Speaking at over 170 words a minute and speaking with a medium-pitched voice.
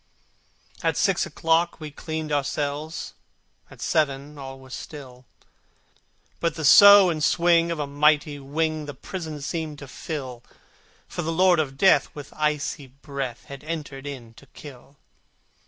No: average, 150 wpm; medium, 150 Hz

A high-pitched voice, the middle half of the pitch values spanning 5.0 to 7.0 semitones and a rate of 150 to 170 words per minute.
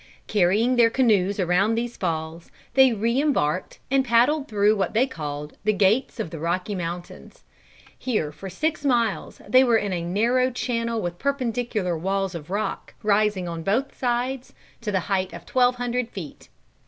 Yes: high, 210 Hz; average, 5.3 semitones; average, 165 wpm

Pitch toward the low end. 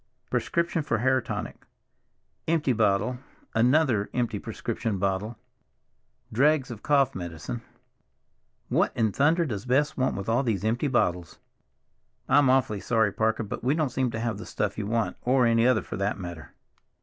Yes: low, 115 Hz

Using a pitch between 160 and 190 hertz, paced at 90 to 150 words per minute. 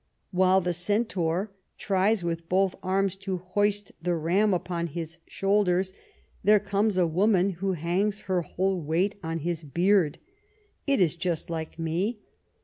Yes: medium, 185 Hz; average, 145 wpm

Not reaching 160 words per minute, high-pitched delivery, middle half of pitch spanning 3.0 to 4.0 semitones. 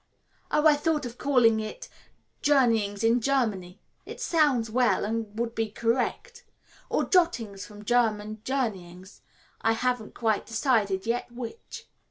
Yes: slow, 135 wpm; high, 230 Hz; average, 3.3 semitones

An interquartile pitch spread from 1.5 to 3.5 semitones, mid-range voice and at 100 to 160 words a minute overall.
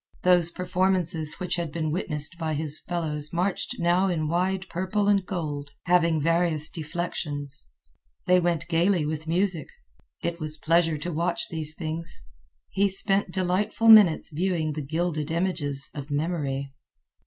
Yes: average, 2.8 semitones; medium, 170 Hz; average, 140 wpm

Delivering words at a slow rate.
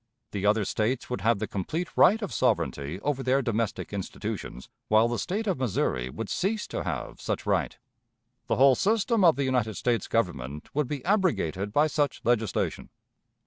No: average, 175 wpm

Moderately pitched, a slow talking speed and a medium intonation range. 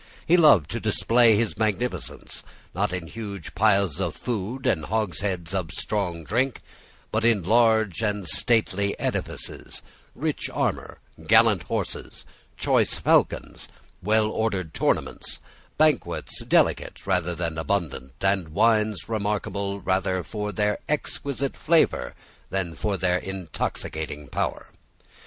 No: low, 100 Hz; slow, 120 wpm; average, 3.6 semitones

